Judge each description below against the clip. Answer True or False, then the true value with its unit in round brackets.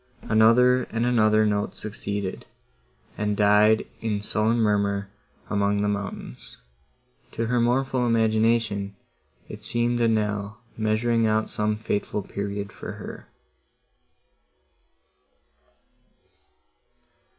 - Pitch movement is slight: True (2.0 semitones)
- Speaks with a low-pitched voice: True (110 Hz)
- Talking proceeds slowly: True (95 wpm)